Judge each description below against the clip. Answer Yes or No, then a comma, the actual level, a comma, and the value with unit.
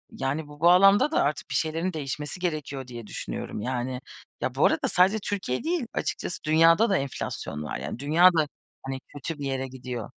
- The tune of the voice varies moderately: Yes, average, 5.0 semitones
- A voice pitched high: No, medium, 150 Hz